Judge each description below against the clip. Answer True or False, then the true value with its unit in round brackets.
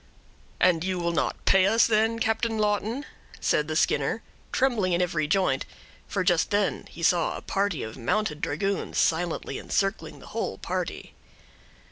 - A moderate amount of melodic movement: True (4.3 semitones)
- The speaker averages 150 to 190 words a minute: True (155 wpm)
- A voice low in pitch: False (185 Hz)